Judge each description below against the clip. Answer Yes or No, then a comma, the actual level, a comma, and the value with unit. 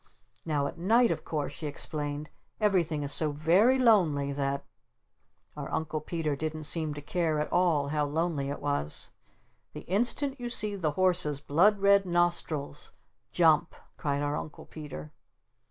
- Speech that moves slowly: No, average, 155 wpm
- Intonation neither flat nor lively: Yes, average, 3.7 semitones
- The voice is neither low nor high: Yes, medium, 155 Hz